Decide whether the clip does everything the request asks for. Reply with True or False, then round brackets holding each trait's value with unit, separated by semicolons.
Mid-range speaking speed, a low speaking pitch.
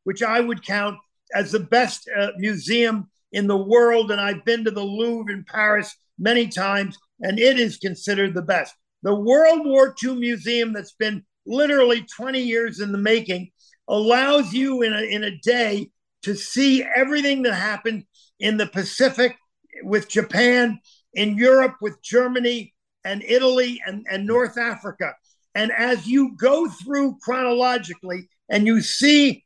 False (155 wpm; 225 Hz)